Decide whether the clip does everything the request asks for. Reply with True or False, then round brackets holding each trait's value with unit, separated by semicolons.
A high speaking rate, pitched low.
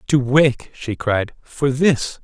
False (160 wpm; 130 Hz)